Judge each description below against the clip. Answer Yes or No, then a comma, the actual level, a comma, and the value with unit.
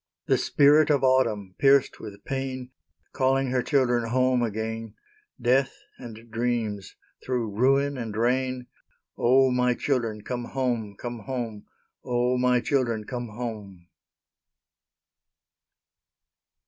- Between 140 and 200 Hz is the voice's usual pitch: No, low, 125 Hz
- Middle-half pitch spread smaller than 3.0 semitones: Yes, narrow, 2.6 semitones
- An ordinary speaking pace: No, slow, 110 wpm